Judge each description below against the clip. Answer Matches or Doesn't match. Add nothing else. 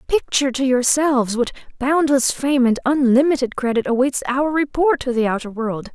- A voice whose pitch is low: Doesn't match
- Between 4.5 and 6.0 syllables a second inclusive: Matches